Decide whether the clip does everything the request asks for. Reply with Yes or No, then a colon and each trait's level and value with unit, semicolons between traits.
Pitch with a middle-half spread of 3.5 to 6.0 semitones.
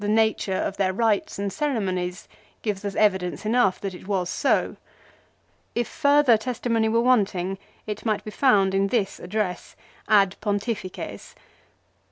No: average, 2.9 semitones